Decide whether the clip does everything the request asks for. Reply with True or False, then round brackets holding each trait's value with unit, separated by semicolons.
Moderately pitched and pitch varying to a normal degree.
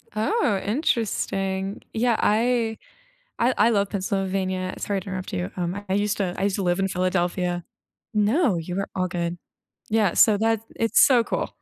False (195 Hz; 3.2 semitones)